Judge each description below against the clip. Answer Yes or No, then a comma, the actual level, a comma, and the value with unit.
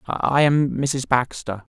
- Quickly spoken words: No, slow, 135 wpm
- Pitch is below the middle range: Yes, low, 130 Hz